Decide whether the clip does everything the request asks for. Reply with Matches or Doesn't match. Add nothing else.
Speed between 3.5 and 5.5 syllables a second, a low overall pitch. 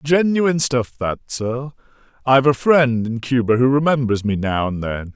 Matches